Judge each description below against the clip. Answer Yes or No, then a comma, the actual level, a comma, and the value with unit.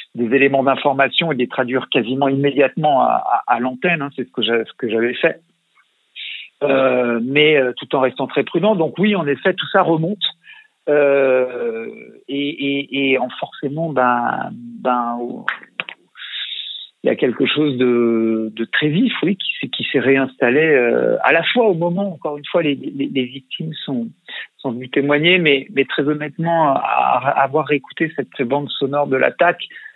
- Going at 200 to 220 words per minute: No, average, 175 wpm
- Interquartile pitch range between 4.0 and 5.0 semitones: Yes, average, 4.4 semitones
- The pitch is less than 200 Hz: Yes, medium, 140 Hz